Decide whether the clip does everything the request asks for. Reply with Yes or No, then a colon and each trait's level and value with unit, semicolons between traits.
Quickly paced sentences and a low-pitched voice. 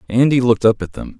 Yes: fast, 250 wpm; low, 120 Hz